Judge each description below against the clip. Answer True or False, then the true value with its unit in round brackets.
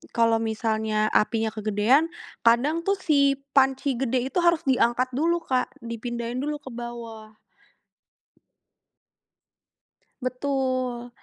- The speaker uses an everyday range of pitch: True (3.2 semitones)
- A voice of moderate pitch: False (250 Hz)